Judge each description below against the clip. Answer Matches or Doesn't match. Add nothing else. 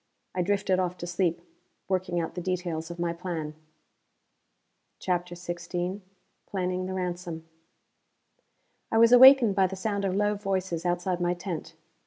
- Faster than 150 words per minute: Doesn't match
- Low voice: Doesn't match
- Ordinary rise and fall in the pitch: Doesn't match